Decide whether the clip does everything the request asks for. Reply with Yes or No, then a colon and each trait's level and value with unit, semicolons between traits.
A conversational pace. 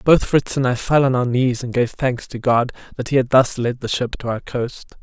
No: fast, 275 wpm